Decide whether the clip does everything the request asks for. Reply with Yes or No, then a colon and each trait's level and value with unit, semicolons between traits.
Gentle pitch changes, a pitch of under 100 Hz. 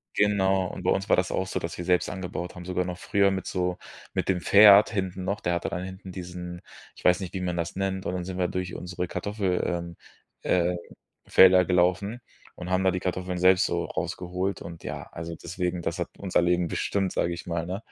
Yes: narrow, 1.3 semitones; very low, 90 Hz